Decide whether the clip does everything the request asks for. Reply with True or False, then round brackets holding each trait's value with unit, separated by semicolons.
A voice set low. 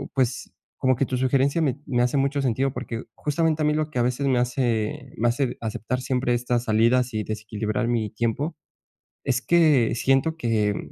True (125 Hz)